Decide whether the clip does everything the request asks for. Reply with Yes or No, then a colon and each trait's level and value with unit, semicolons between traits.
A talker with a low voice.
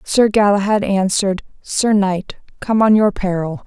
No: high, 200 Hz